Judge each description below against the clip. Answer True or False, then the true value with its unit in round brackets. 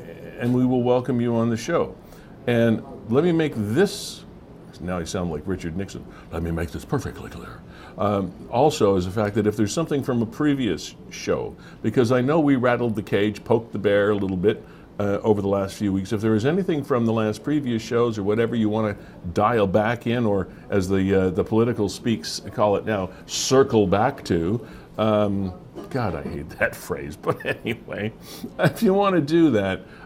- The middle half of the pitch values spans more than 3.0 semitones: True (3.5 semitones)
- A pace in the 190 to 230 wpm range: True (200 wpm)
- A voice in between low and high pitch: False (110 Hz)